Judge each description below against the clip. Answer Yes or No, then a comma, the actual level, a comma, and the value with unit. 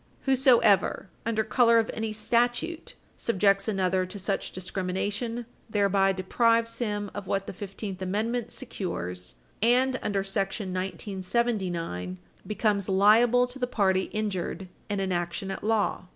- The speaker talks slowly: Yes, slow, 130 wpm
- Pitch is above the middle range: Yes, high, 205 Hz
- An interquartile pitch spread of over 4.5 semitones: No, average, 3.4 semitones